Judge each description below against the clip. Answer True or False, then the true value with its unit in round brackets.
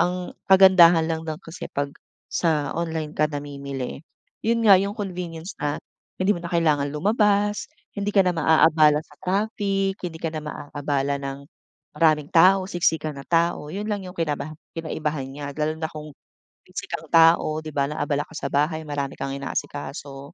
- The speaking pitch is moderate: True (160 Hz)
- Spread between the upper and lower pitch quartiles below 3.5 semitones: False (3.8 semitones)